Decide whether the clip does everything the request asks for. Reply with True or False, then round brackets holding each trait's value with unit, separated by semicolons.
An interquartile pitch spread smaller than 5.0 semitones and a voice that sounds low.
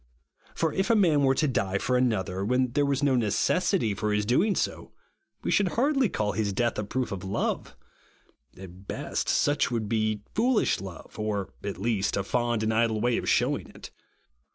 False (5.5 semitones; 115 Hz)